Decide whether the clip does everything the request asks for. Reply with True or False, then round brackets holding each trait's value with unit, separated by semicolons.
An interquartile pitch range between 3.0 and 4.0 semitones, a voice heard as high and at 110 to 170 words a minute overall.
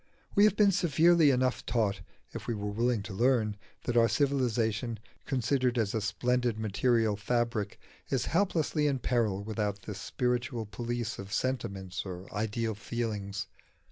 False (3.5 semitones; 115 Hz; 145 wpm)